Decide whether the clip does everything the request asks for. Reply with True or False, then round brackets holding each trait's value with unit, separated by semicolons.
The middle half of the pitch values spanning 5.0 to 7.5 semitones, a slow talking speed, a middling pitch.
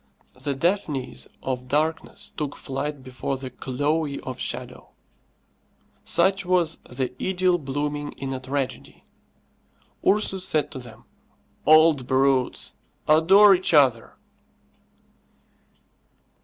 False (3.8 semitones; 100 wpm; 145 Hz)